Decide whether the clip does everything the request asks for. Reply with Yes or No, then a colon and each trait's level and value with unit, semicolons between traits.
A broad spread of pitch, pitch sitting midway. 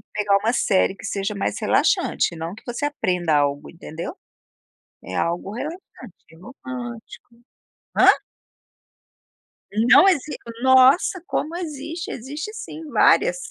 No: wide, 7.6 semitones; high, 245 Hz